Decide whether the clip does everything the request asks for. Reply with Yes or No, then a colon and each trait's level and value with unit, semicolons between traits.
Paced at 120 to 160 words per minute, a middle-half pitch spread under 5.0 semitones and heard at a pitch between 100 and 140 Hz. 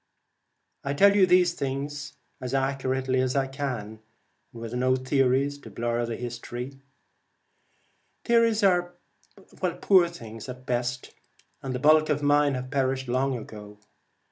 Yes: average, 140 wpm; average, 2.8 semitones; low, 135 Hz